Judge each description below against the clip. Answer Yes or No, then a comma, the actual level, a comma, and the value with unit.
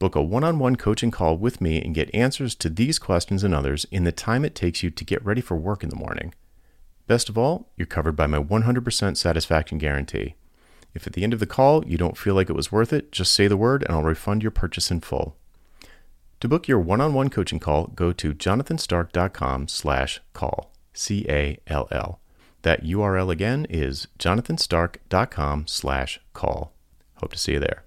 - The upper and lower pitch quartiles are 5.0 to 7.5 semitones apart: Yes, wide, 5.5 semitones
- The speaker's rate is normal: Yes, average, 190 wpm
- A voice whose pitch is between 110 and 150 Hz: No, very low, 90 Hz